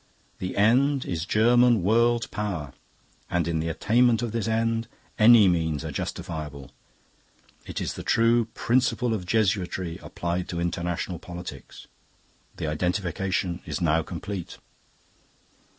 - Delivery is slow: Yes, slow, 125 wpm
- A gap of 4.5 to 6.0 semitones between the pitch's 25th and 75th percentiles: Yes, average, 5.0 semitones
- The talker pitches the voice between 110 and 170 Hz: No, very low, 95 Hz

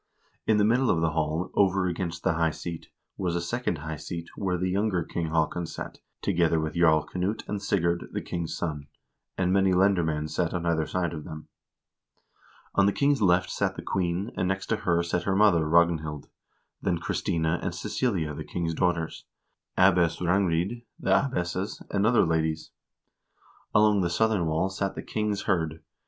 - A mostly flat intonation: No, average, 3.0 semitones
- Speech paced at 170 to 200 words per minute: Yes, average, 175 wpm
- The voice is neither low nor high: No, very low, 85 Hz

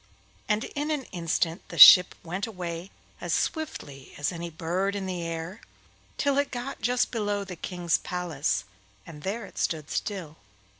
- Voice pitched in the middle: Yes, medium, 180 Hz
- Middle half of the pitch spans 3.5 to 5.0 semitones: Yes, average, 4.1 semitones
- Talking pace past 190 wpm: No, average, 160 wpm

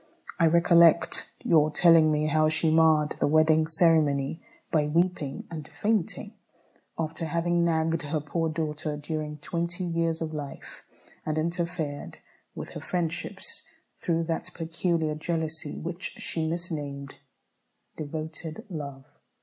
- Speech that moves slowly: Yes, slow, 125 wpm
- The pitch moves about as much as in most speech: No, narrow, 1.6 semitones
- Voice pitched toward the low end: No, medium, 160 Hz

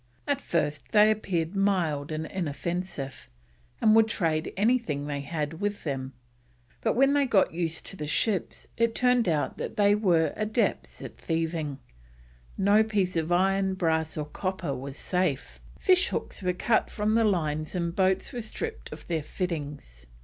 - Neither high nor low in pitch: Yes, medium, 180 Hz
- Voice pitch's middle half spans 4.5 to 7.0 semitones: Yes, average, 5.2 semitones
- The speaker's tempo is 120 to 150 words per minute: No, average, 165 wpm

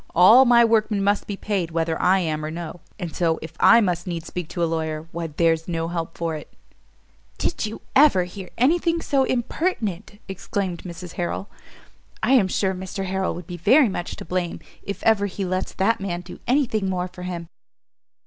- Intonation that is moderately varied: Yes, average, 3.8 semitones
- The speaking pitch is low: No, medium, 185 Hz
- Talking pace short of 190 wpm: No, average, 200 wpm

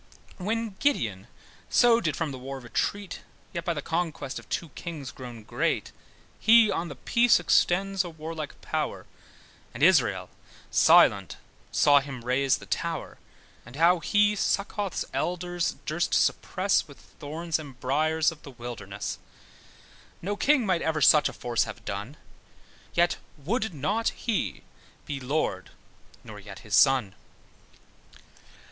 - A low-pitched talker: No, medium, 160 Hz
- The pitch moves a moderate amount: No, wide, 5.8 semitones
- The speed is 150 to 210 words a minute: No, average, 140 wpm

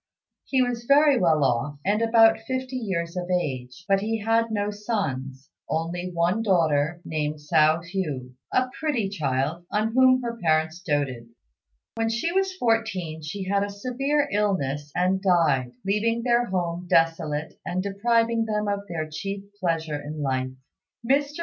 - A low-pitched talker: No, medium, 185 Hz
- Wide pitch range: Yes, wide, 6.3 semitones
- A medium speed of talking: Yes, average, 155 wpm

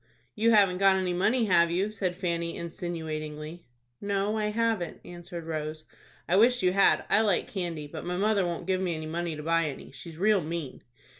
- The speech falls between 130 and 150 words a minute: No, average, 190 wpm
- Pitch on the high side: No, medium, 175 Hz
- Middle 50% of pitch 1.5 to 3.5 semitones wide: Yes, average, 3.2 semitones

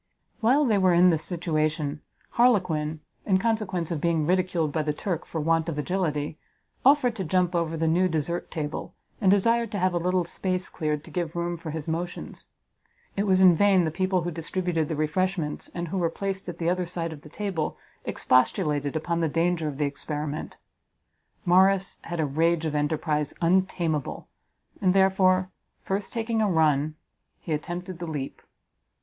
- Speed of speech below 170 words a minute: No, average, 180 wpm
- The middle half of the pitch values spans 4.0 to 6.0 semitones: No, average, 3.2 semitones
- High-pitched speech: No, medium, 170 Hz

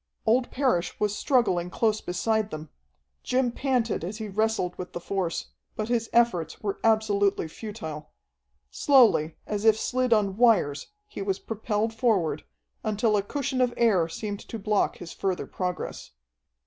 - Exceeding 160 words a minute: No, average, 150 wpm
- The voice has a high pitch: Yes, high, 210 Hz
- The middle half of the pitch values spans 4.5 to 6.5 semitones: No, average, 4.0 semitones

